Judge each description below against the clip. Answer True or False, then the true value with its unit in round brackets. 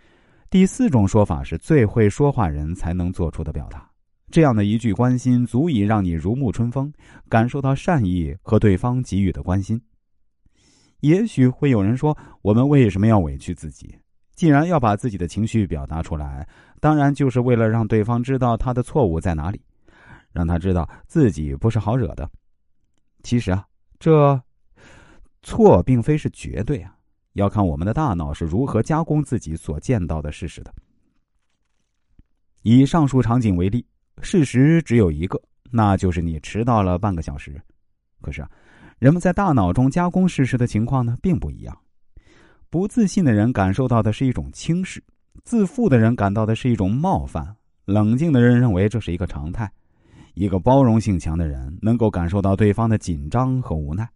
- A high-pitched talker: False (110 Hz)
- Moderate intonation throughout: False (6.4 semitones)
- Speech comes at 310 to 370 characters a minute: False (265 characters per minute)